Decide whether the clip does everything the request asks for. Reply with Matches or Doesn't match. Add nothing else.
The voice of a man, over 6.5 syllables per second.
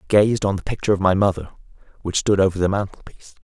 Matches